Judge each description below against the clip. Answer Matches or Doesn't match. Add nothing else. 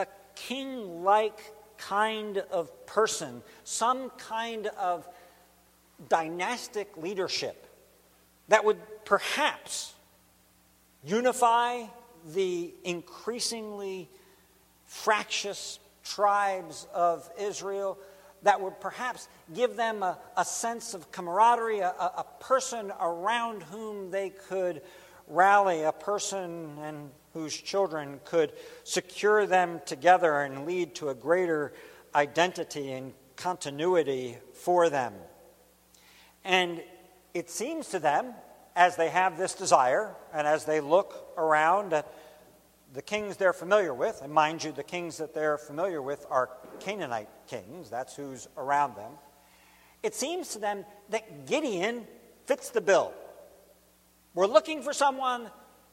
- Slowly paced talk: Matches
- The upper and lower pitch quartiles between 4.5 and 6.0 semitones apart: Matches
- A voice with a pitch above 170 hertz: Matches